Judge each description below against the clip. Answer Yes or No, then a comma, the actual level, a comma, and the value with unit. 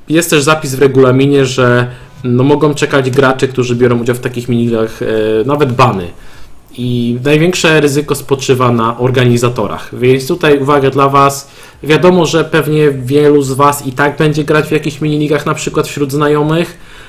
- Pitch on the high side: No, medium, 140 Hz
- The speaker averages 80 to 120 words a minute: No, fast, 160 wpm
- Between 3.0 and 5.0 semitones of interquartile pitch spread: Yes, average, 3.3 semitones